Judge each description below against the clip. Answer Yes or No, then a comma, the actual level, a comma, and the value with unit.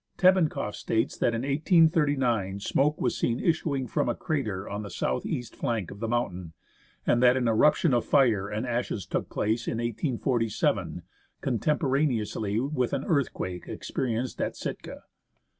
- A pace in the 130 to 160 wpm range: Yes, average, 150 wpm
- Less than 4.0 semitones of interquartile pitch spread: No, average, 4.3 semitones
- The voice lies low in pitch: Yes, low, 120 Hz